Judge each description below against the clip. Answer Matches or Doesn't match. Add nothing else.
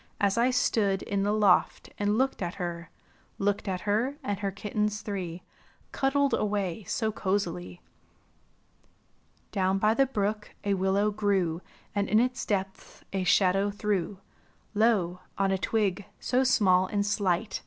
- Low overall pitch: Doesn't match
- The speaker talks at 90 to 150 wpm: Matches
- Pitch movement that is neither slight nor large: Doesn't match